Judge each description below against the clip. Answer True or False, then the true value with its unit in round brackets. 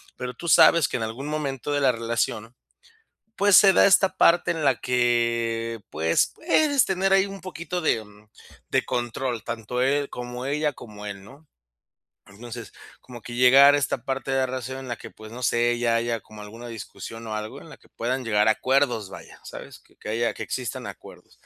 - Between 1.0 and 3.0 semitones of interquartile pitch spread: False (3.7 semitones)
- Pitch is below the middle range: True (125 Hz)